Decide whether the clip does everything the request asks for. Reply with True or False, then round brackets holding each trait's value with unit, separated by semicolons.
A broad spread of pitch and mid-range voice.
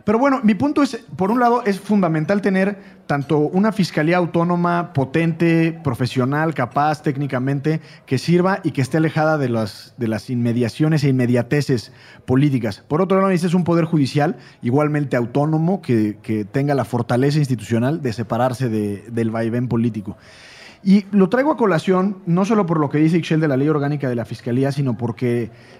True (6.0 semitones; 150 Hz)